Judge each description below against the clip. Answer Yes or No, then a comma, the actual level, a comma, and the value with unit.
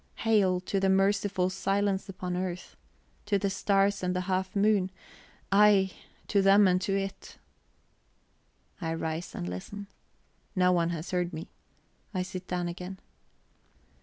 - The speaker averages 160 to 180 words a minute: No, average, 140 wpm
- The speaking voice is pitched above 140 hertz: Yes, high, 190 Hz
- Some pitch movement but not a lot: No, narrow, 1.6 semitones